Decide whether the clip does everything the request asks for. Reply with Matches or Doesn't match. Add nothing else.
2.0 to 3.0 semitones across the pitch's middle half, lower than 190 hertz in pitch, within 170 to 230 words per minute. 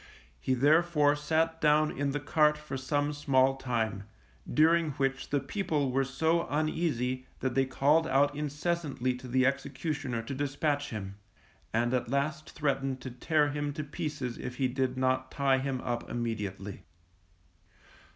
Doesn't match